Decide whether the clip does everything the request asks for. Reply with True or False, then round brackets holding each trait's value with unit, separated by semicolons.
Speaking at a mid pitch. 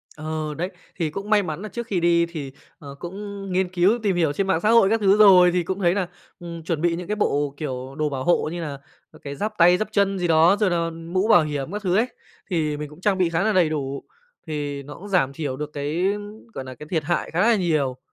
True (170 Hz)